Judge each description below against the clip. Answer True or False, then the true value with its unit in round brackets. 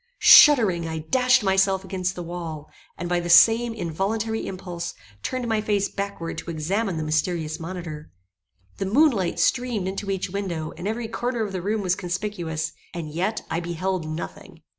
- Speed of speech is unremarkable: True (170 wpm)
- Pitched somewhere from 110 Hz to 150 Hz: False (185 Hz)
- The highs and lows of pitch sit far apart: False (4.0 semitones)